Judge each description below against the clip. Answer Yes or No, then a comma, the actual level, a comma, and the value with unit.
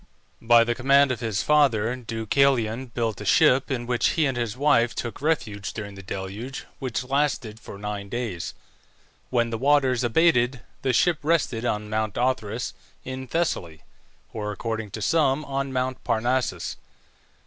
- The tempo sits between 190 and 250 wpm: No, average, 155 wpm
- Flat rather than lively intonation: No, average, 3.4 semitones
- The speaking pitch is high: No, low, 120 Hz